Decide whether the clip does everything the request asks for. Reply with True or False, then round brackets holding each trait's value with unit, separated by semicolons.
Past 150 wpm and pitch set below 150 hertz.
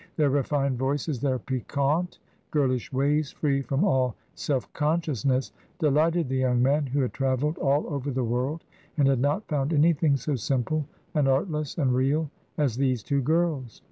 True (165 wpm; 140 Hz)